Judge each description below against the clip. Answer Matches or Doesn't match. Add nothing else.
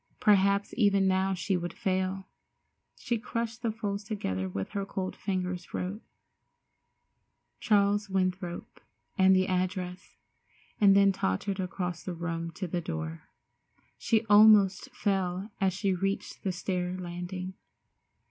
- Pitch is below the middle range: Doesn't match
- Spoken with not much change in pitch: Matches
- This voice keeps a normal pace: Doesn't match